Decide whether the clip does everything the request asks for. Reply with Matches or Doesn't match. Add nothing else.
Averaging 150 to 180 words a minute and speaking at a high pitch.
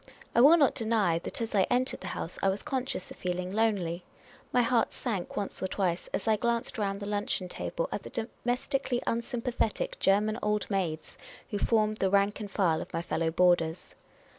Doesn't match